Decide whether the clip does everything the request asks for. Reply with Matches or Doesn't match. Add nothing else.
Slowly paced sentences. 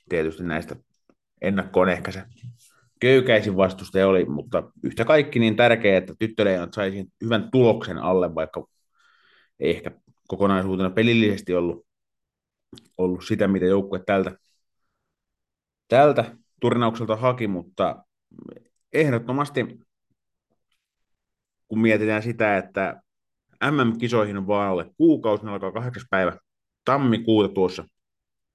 Doesn't match